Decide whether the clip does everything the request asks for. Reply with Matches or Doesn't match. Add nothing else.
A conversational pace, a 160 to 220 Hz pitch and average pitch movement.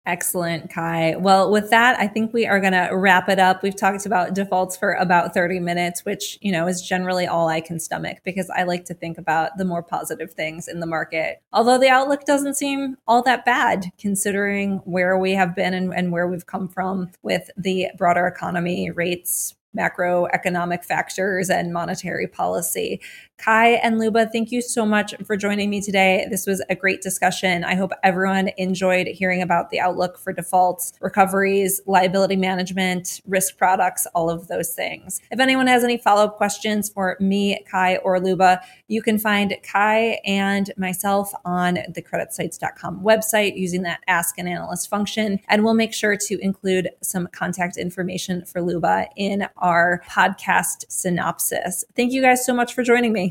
Doesn't match